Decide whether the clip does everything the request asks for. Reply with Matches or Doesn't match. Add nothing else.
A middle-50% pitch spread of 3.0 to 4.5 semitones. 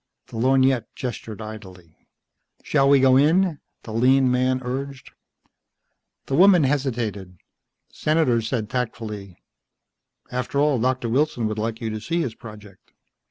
Matches